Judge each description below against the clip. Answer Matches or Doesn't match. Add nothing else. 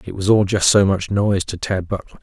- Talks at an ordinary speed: Doesn't match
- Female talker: Doesn't match